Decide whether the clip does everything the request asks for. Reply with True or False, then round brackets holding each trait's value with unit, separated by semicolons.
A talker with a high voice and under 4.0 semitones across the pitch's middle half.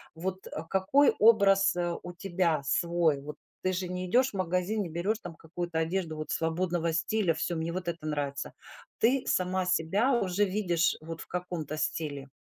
False (175 Hz; 2.8 semitones)